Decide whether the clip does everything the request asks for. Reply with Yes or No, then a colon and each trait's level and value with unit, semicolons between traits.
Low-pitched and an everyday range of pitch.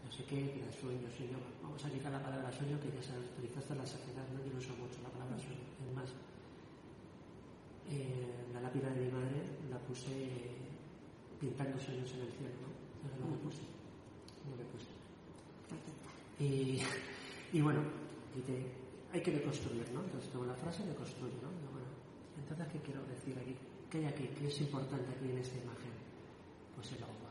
No: low, 130 Hz; narrow, 1.8 semitones